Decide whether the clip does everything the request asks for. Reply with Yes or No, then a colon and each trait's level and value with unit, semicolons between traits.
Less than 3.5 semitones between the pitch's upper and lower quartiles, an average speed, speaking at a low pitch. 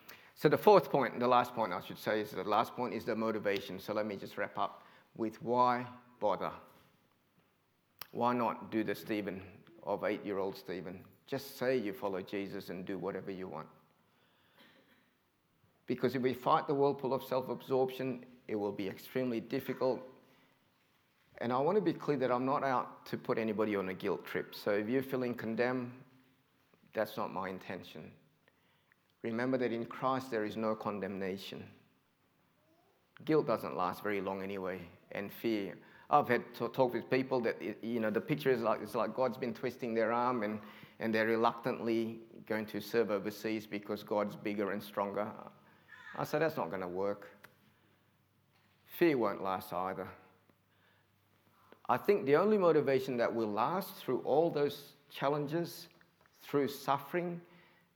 No: average, 4.2 semitones; average, 165 wpm; low, 115 Hz